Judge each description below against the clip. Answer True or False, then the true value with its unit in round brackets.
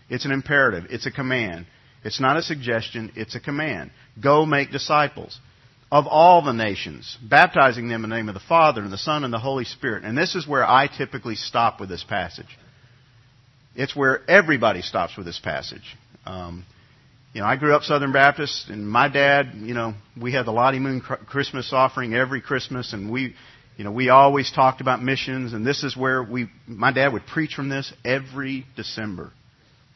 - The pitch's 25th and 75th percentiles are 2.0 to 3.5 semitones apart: True (3.0 semitones)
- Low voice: True (130 Hz)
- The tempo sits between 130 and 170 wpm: False (190 wpm)